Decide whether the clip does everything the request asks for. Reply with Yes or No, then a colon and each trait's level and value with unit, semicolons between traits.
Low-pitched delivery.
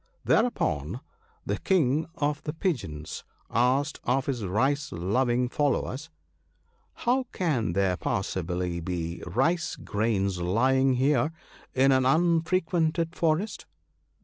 Yes: low, 130 Hz